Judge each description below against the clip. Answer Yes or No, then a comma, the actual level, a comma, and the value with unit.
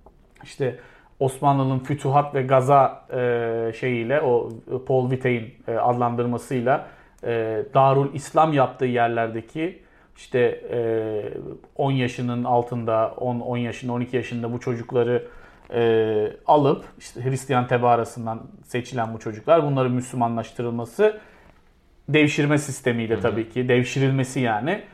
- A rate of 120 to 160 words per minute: No, slow, 95 wpm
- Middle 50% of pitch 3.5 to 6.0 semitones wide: No, narrow, 2.4 semitones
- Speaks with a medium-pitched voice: No, low, 125 Hz